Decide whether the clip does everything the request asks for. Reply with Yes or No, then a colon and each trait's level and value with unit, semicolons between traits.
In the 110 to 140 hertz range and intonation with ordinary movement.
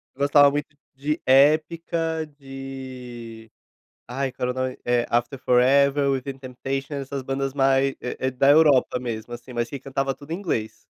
No: low, 135 Hz; narrow, 2.1 semitones